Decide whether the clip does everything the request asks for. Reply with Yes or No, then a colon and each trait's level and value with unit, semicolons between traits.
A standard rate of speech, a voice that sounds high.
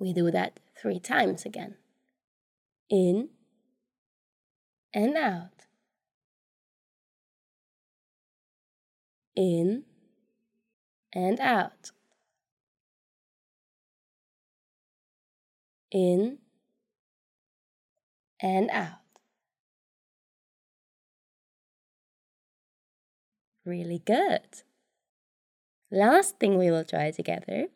No: slow, 50 wpm; high, 215 Hz